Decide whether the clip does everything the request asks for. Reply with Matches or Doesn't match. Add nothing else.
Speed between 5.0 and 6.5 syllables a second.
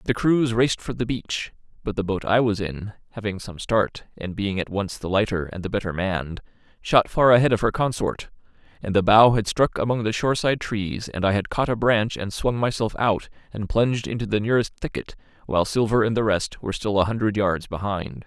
Matches